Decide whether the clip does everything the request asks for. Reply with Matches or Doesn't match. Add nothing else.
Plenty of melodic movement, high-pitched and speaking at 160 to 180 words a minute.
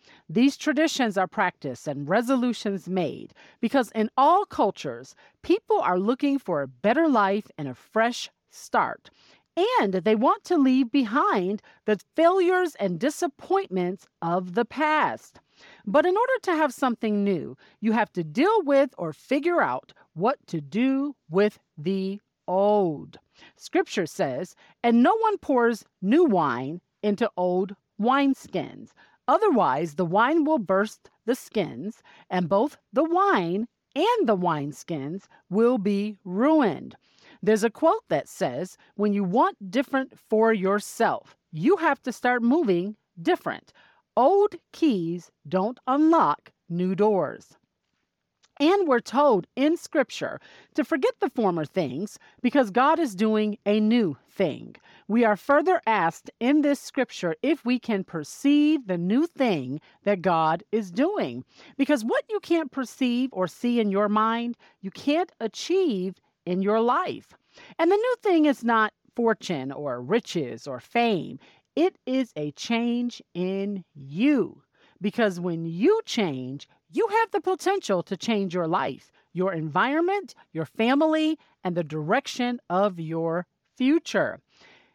Doesn't match